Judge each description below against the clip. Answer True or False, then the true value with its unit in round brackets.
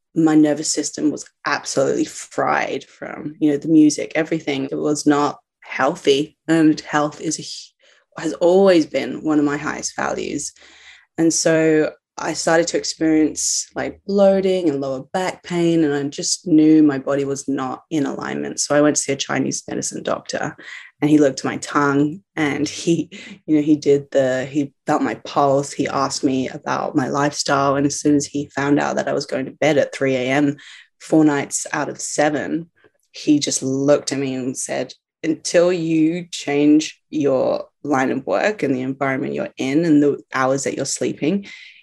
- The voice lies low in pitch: False (150 Hz)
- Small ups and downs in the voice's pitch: True (2.3 semitones)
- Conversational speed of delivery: True (185 wpm)